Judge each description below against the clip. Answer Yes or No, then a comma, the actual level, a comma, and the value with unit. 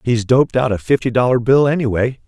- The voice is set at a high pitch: No, low, 125 Hz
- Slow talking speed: No, fast, 210 wpm